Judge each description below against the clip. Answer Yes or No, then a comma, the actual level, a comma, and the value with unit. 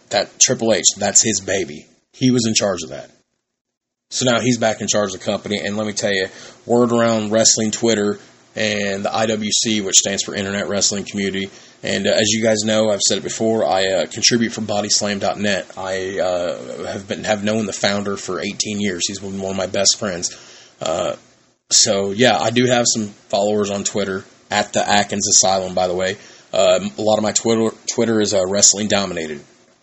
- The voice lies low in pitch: Yes, low, 105 Hz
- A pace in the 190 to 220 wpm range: Yes, average, 200 wpm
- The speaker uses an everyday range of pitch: No, narrow, 1.9 semitones